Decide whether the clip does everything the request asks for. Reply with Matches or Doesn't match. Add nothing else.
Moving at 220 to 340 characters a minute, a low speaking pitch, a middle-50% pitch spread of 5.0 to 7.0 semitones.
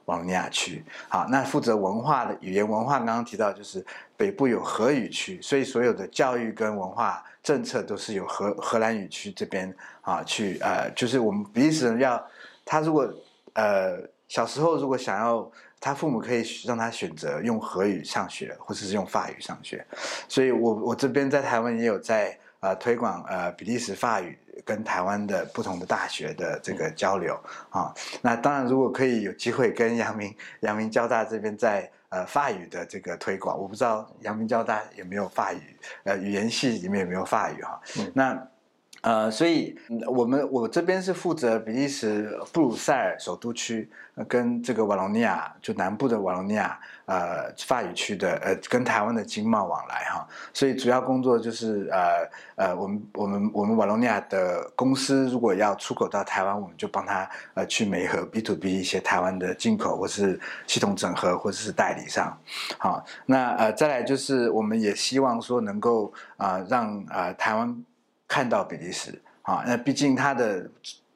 Doesn't match